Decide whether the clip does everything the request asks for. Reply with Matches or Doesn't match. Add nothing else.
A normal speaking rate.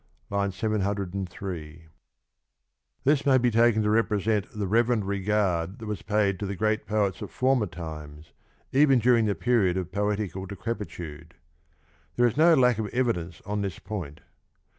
Matches